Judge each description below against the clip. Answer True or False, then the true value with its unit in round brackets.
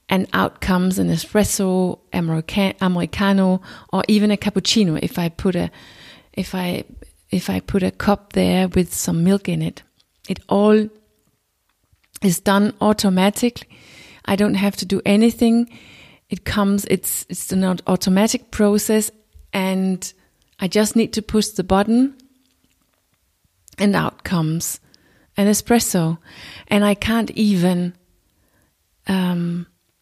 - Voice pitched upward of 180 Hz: True (190 Hz)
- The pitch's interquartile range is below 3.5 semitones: True (2.8 semitones)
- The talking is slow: True (125 wpm)